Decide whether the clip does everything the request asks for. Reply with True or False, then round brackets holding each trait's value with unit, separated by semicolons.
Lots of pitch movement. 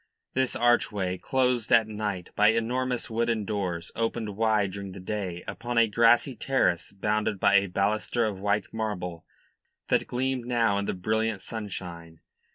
False (2.9 semitones)